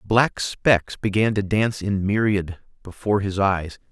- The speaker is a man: Yes, male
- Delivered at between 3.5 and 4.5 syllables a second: Yes, 4.4 syllables/s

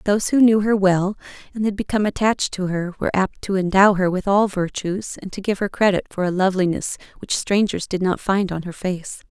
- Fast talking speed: Yes, fast, 225 wpm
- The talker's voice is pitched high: Yes, high, 195 Hz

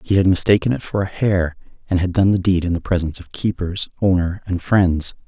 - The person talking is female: No, male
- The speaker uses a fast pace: Yes, fast, 225 wpm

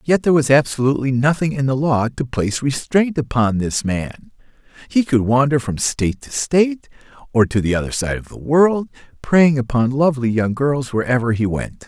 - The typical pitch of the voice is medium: No, low, 130 Hz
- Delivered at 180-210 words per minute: Yes, average, 185 wpm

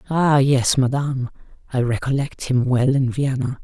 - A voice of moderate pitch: No, low, 130 Hz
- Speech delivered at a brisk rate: No, average, 150 wpm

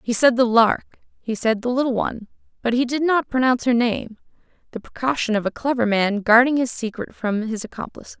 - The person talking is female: Yes, female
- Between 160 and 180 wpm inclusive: No, average, 200 wpm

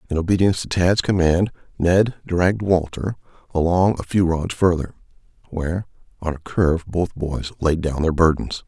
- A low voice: Yes, very low, 85 Hz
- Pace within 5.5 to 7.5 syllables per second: No, 5.1 syllables/s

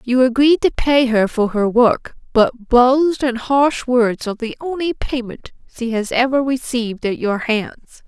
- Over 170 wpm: Yes, average, 180 wpm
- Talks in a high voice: Yes, high, 245 Hz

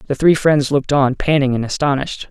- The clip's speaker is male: Yes, male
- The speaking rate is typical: No, fast, 210 wpm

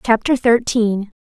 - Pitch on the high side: Yes, high, 225 Hz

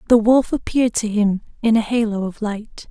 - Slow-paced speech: No, fast, 205 wpm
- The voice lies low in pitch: No, high, 220 Hz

